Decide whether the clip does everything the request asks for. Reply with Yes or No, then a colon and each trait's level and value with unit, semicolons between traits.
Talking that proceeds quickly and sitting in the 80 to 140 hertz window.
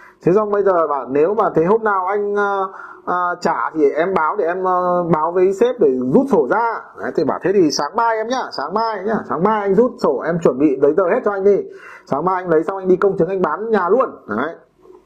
No: fast, 265 wpm; high, 210 Hz